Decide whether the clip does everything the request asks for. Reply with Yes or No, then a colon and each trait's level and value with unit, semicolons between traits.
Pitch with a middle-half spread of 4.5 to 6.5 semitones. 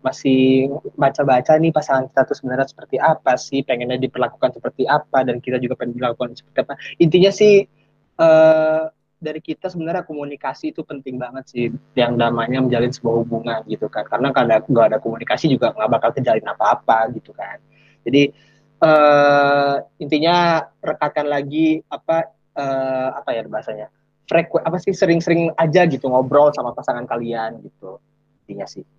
No: average, 3.9 semitones